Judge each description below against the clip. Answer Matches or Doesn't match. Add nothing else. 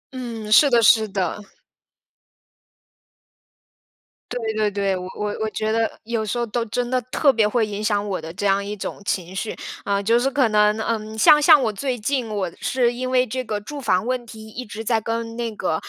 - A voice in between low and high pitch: Doesn't match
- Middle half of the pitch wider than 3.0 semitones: Doesn't match